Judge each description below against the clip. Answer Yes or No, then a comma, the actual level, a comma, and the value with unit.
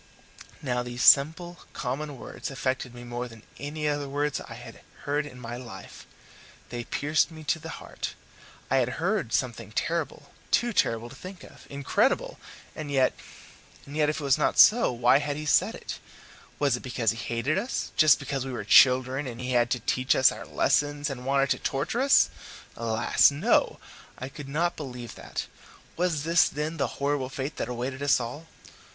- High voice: No, medium, 140 Hz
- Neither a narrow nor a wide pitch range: Yes, average, 3.5 semitones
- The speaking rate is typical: Yes, average, 185 wpm